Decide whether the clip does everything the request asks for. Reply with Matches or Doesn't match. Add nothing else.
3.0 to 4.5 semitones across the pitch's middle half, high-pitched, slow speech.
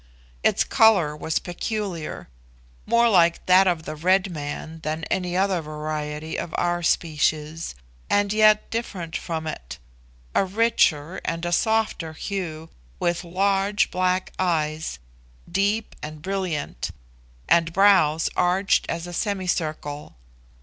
Doesn't match